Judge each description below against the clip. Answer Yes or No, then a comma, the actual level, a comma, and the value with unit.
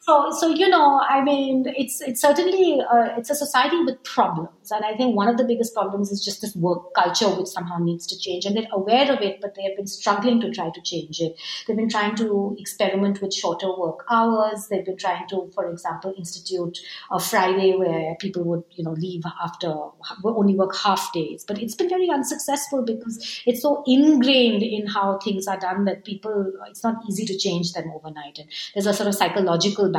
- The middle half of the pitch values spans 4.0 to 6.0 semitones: Yes, average, 4.5 semitones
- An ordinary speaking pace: No, fast, 210 wpm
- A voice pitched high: Yes, high, 200 Hz